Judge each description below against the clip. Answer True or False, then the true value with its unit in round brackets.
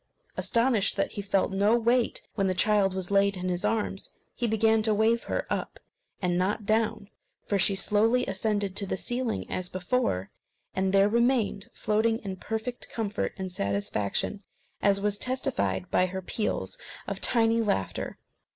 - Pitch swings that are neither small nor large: True (3.0 semitones)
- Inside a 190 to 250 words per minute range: False (160 wpm)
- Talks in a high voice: True (205 Hz)